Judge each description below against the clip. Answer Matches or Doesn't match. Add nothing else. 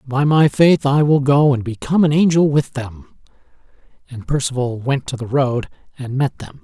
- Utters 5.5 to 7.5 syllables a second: Doesn't match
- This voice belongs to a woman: Doesn't match